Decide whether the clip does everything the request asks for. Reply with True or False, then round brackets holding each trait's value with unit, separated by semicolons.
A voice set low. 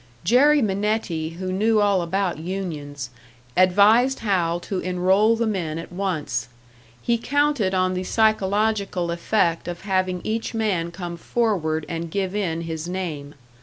False (185 Hz)